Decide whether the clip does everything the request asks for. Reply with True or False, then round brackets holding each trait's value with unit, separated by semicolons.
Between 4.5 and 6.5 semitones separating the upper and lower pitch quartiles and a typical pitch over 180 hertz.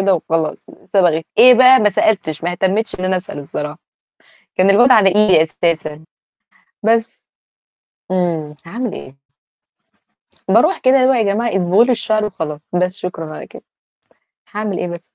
True (5.1 semitones; 190 Hz)